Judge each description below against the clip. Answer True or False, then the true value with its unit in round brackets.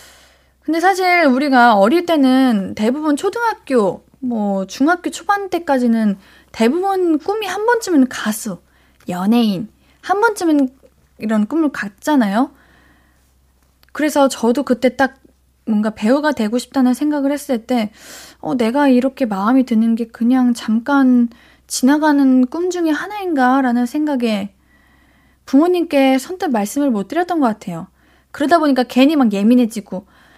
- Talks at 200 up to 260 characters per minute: False (280 characters per minute)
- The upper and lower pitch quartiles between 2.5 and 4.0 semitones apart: False (5.2 semitones)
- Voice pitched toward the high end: True (260 Hz)